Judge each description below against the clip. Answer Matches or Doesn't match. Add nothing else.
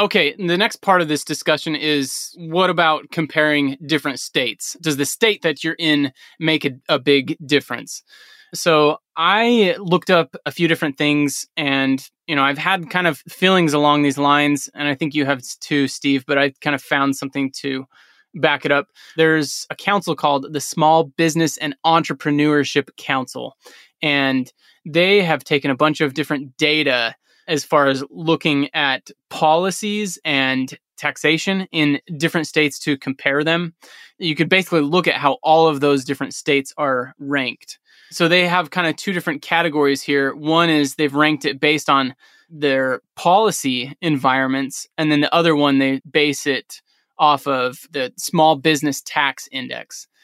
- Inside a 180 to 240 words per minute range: Doesn't match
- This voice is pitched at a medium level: Matches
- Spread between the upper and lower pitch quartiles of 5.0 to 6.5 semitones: Doesn't match